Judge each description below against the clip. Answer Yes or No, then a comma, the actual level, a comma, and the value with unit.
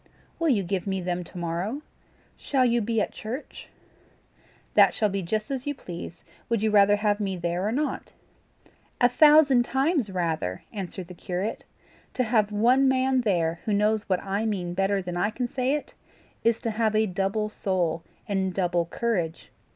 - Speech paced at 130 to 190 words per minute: Yes, average, 180 wpm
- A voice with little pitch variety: No, average, 4.6 semitones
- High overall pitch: Yes, high, 205 Hz